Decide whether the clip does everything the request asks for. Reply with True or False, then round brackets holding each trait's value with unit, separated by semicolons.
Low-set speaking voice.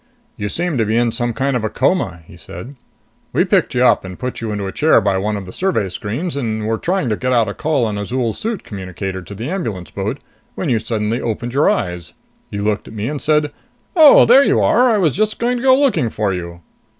True (115 Hz)